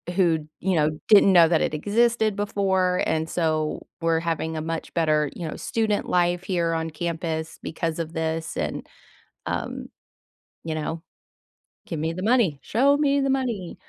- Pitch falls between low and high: Yes, medium, 170 Hz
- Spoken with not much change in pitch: No, average, 3.8 semitones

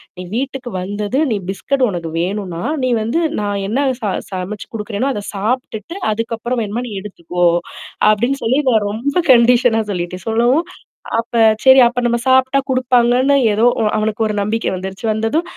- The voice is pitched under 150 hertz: No, high, 225 Hz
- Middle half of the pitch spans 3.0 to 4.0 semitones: Yes, average, 3.6 semitones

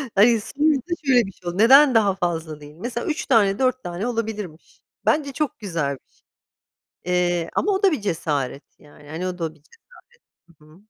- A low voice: No, high, 195 Hz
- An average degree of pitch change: No, wide, 7.1 semitones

